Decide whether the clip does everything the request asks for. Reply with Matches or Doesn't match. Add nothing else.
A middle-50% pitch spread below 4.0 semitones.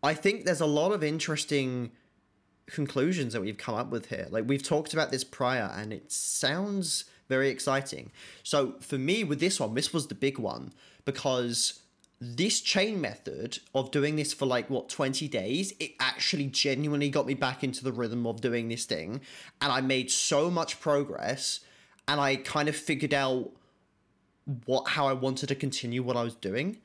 Matches